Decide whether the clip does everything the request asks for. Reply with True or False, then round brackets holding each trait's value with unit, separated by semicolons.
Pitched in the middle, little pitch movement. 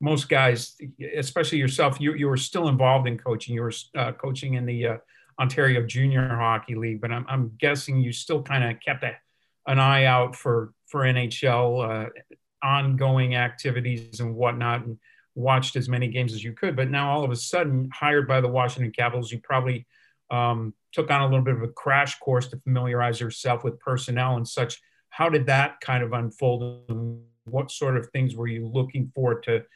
False (125 Hz; 2.1 semitones)